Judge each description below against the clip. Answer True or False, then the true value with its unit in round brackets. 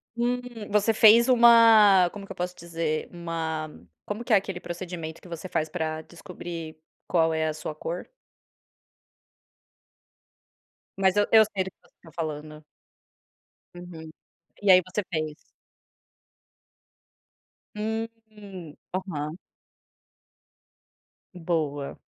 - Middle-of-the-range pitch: True (175 Hz)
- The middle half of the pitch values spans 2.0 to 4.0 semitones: False (4.5 semitones)